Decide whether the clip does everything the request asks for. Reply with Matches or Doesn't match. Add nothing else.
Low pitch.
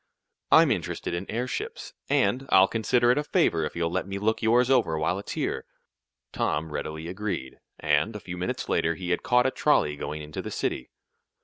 Matches